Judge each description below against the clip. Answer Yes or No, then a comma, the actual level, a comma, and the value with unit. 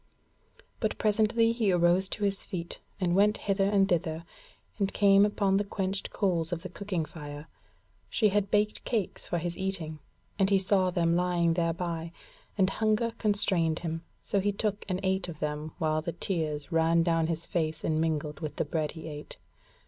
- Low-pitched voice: No, medium, 180 Hz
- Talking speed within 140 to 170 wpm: No, average, 180 wpm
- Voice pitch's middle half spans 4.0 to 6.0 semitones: No, average, 3.4 semitones